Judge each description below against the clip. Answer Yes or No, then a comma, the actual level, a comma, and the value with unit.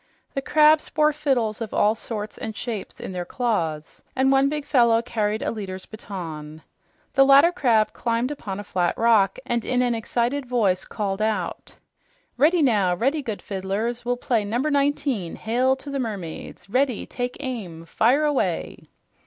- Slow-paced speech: No, average, 165 wpm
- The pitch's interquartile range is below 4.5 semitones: No, average, 4.8 semitones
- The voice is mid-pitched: No, high, 235 Hz